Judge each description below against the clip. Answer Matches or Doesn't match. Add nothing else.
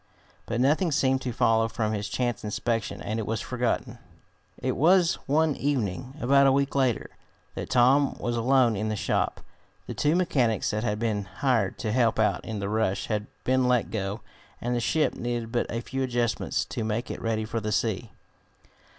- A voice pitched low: Matches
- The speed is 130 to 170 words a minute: Doesn't match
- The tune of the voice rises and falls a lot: Doesn't match